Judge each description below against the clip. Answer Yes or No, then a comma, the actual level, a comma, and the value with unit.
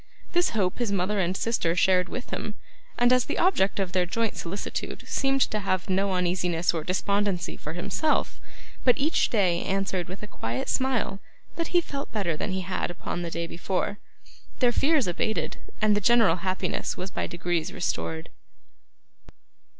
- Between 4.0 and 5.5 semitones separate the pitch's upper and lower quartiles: Yes, average, 4.3 semitones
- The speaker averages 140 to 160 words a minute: No, average, 170 wpm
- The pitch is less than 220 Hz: Yes, high, 190 Hz